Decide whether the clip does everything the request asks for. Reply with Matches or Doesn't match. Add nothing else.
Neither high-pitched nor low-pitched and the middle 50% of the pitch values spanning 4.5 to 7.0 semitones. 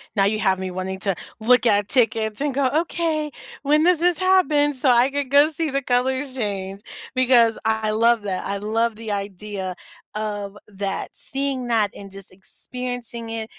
Doesn't match